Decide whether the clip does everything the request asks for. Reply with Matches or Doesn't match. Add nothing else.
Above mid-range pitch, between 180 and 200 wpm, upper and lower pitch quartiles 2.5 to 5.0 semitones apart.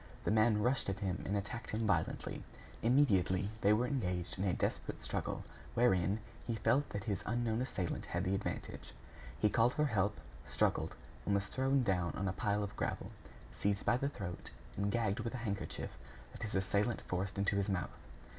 Doesn't match